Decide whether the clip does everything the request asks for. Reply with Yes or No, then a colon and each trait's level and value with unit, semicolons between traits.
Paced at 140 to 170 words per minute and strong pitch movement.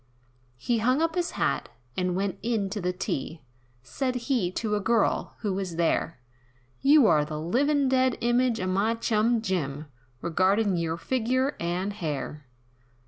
Yes: average, 150 wpm; wide, 5.9 semitones